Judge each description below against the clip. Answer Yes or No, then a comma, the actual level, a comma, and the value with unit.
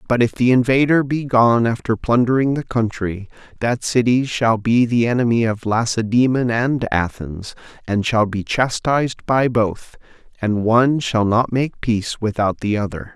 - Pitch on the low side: Yes, low, 115 Hz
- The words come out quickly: No, average, 160 wpm